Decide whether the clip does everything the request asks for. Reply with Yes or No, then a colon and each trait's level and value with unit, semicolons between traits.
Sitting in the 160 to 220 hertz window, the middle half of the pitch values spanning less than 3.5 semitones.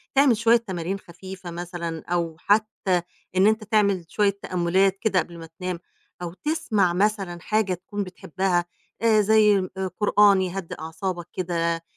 Yes: high, 190 Hz; average, 3.1 semitones